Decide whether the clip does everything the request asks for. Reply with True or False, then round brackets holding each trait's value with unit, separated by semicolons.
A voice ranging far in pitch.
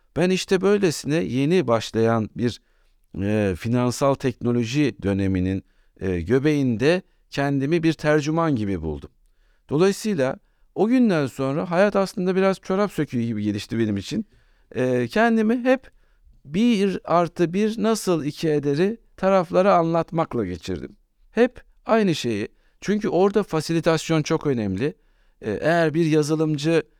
True (7.6 semitones)